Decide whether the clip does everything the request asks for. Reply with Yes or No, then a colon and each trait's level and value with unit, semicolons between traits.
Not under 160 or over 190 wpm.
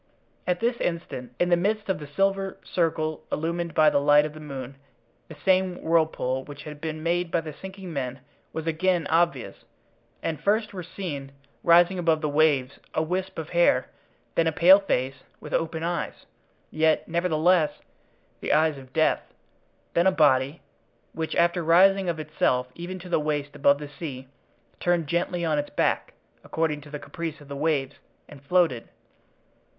Yes: average, 170 wpm